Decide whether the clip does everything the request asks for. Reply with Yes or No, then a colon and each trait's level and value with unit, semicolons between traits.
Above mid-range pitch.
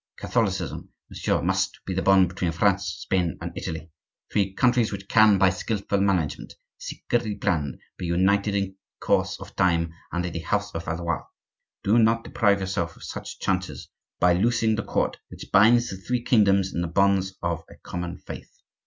No: very low, 95 Hz